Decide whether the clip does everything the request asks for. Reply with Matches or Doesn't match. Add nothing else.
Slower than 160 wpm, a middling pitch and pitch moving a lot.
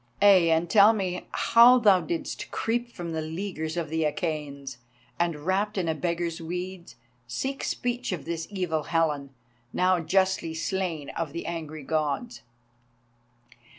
Doesn't match